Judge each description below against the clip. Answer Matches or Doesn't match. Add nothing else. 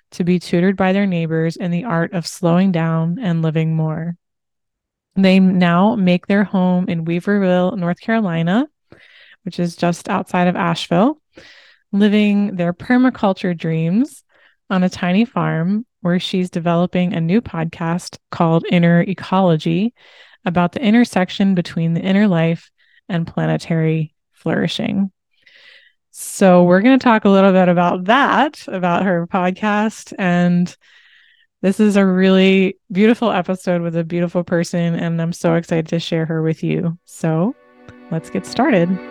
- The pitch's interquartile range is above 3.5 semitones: Doesn't match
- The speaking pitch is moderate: Matches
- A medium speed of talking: Matches